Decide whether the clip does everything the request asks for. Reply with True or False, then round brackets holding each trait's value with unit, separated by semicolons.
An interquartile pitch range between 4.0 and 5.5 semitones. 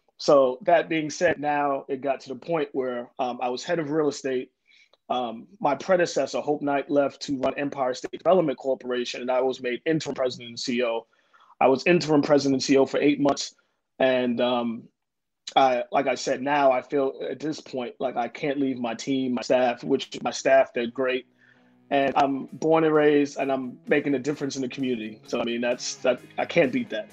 False (2.5 semitones)